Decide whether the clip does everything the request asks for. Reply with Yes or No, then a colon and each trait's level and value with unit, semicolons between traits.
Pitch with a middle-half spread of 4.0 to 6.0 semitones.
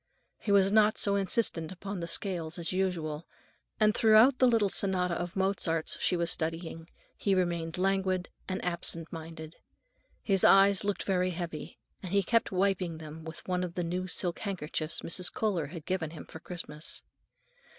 No: average, 2.9 semitones